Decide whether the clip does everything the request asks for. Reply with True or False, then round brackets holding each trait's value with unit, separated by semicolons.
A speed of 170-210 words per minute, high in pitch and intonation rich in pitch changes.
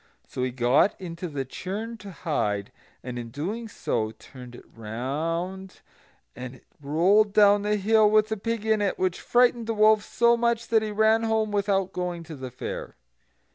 True (180 wpm; 195 Hz; 7.6 semitones)